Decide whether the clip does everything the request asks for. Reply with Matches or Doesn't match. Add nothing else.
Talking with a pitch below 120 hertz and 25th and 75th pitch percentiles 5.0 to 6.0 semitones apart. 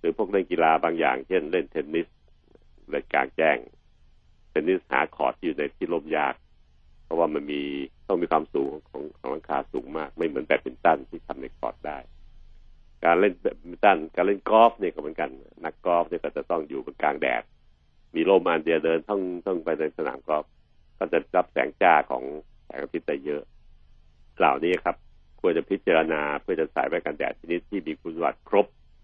Doesn't match